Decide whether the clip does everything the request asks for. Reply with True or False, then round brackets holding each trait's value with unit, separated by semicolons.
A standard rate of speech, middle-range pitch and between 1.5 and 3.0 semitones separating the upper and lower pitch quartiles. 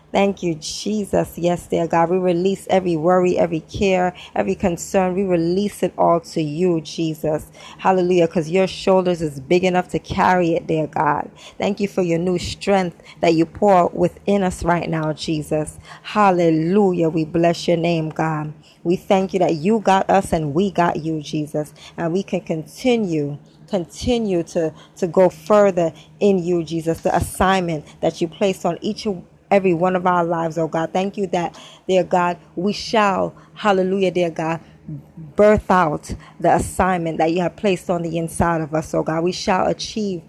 True (180 wpm; 175 Hz; 2.5 semitones)